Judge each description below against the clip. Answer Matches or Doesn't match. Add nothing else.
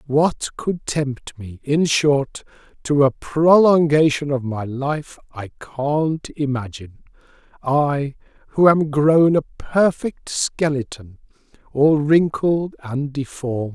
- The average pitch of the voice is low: Doesn't match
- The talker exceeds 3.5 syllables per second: Doesn't match